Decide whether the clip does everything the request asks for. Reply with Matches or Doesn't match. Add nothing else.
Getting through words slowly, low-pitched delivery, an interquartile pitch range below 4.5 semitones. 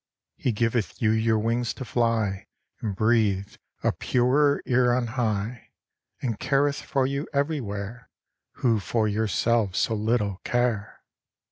Matches